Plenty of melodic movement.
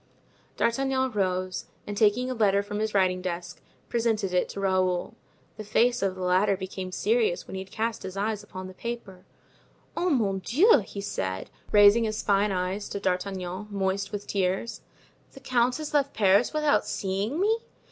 No: average, 3.7 semitones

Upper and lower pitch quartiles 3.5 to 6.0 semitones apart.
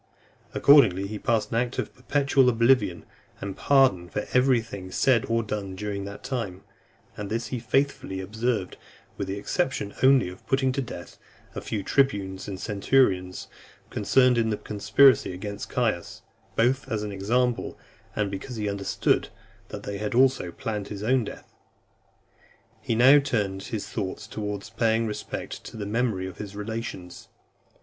Yes: average, 4.1 semitones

